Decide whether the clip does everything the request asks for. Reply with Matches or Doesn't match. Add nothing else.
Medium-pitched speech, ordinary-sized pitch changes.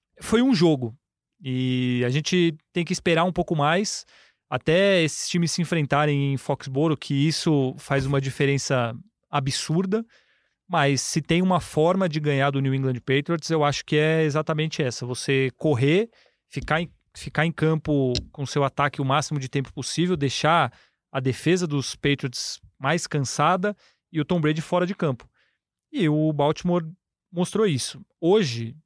Matches